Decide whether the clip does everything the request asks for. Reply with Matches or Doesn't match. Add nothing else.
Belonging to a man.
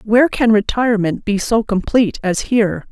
Doesn't match